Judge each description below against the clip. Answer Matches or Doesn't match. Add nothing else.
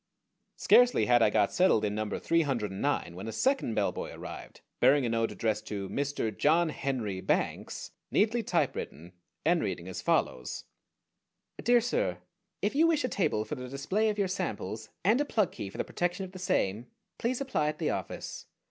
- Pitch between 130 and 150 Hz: Matches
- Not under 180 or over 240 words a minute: Matches